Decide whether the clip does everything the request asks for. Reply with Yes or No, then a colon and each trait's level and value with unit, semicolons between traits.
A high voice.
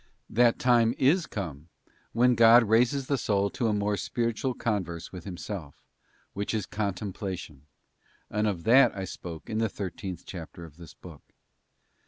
No: low, 105 Hz